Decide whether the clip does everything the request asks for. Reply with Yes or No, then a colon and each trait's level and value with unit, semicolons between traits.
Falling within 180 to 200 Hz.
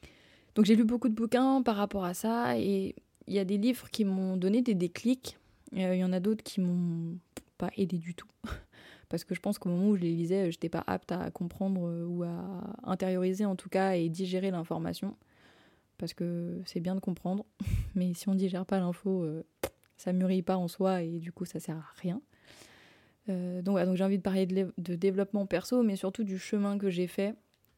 Yes: high, 190 Hz